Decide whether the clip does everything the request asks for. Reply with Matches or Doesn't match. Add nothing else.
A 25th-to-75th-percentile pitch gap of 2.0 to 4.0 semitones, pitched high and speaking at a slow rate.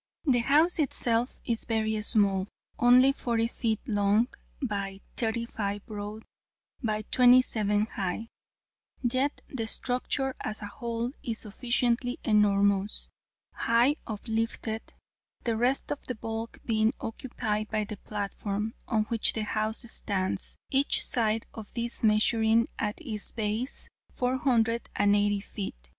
Matches